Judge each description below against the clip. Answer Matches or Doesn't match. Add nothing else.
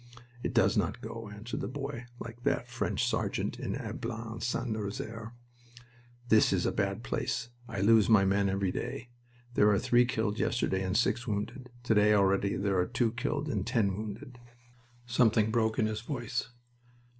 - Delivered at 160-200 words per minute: Matches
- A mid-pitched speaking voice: Doesn't match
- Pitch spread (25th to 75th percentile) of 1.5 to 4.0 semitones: Matches